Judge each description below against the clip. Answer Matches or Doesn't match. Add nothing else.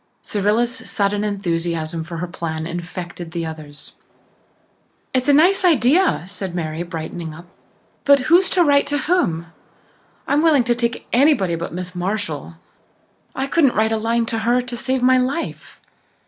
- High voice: Matches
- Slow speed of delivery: Doesn't match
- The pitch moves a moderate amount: Doesn't match